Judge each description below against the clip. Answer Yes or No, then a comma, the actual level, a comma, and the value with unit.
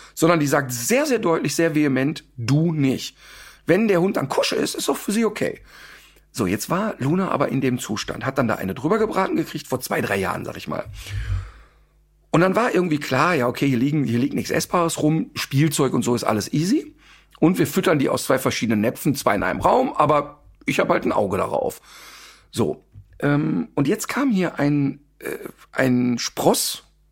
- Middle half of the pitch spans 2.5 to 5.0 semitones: No, wide, 5.4 semitones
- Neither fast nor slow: No, fast, 205 wpm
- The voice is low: No, medium, 145 Hz